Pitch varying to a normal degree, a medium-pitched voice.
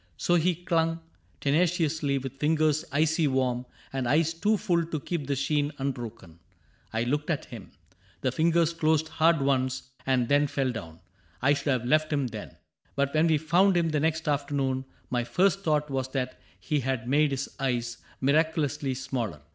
Yes: average, 3.4 semitones; medium, 145 Hz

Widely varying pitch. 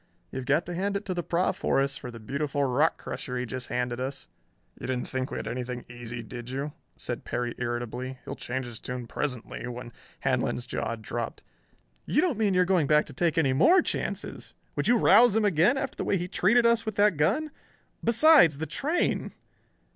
Yes: wide, 7.9 semitones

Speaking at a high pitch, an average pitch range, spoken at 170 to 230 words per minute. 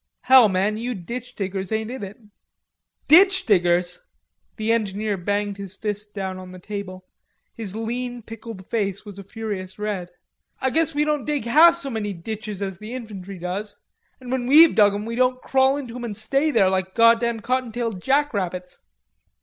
Yes: high, 215 Hz; average, 4.3 semitones; average, 175 wpm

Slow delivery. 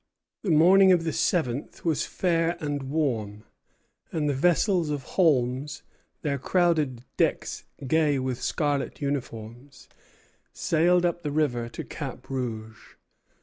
Yes: slow, 125 wpm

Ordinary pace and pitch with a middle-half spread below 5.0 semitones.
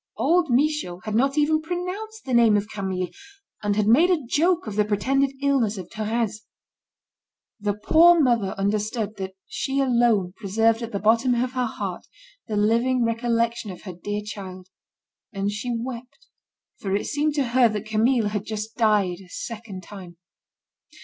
Yes: average, 165 wpm; average, 4.0 semitones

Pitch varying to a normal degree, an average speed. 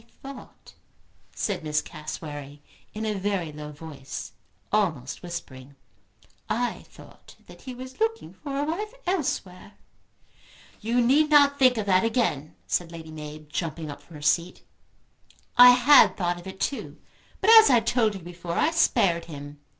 No: wide, 8.4 semitones; average, 160 wpm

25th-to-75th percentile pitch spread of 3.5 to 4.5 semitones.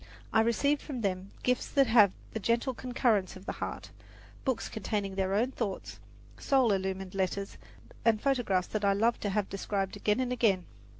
Yes: average, 3.9 semitones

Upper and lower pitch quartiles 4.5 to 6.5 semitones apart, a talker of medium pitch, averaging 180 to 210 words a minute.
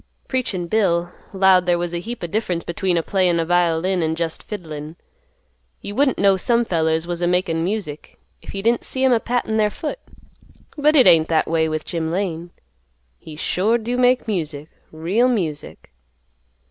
Yes: average, 5.0 semitones; medium, 180 Hz; average, 185 wpm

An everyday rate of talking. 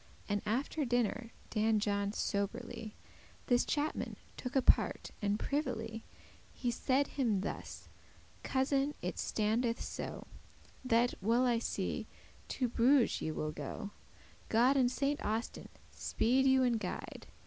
No: slow, 125 wpm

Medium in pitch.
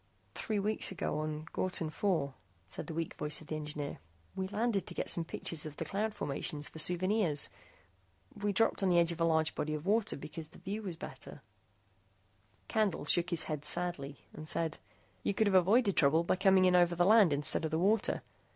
Yes: medium, 170 Hz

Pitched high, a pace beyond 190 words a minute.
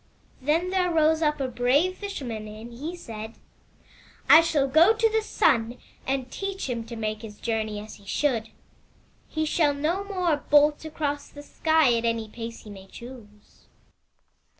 No: very high, 275 Hz; average, 170 wpm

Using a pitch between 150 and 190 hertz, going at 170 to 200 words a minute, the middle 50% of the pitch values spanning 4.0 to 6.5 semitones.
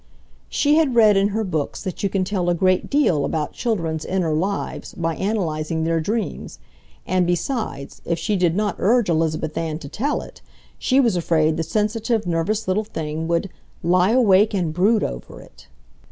Yes: medium, 185 Hz; average, 180 wpm; average, 4.7 semitones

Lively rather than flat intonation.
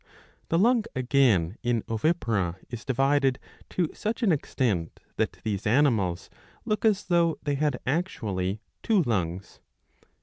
Yes: wide, 8.1 semitones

